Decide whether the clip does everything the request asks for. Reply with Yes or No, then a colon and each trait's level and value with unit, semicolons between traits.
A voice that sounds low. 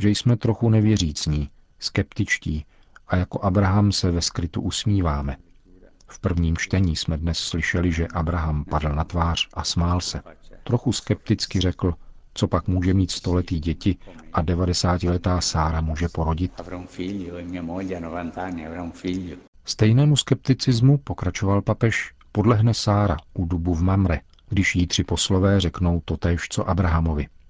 Yes: very low, 90 Hz